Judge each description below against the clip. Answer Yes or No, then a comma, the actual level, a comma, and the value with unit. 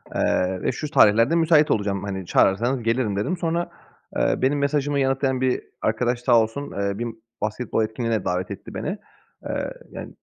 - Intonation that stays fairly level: No, average, 5.1 semitones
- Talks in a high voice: No, low, 120 Hz